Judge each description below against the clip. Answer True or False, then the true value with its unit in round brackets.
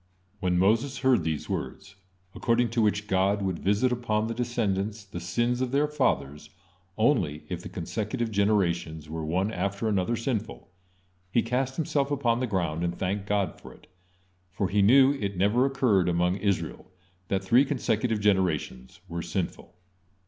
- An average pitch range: True (4.6 semitones)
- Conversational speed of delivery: True (160 wpm)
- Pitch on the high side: False (100 Hz)